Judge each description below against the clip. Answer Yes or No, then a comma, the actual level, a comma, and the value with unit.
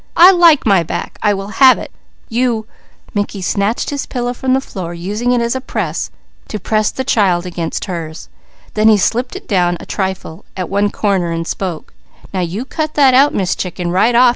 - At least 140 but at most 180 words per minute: No, average, 190 wpm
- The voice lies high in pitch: Yes, high, 205 Hz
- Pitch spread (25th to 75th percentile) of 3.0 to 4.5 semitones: No, average, 5.3 semitones